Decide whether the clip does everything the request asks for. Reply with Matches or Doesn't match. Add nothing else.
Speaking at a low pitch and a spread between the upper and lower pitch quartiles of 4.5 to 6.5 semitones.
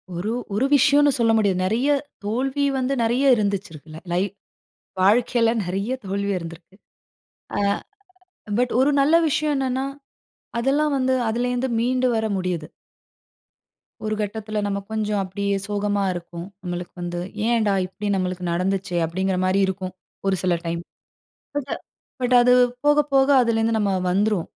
Doesn't match